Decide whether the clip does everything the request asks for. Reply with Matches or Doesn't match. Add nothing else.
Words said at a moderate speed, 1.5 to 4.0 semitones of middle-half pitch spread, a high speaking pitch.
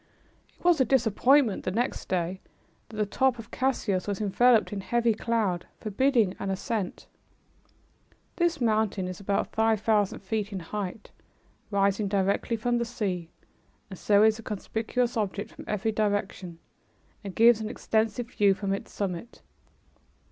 Matches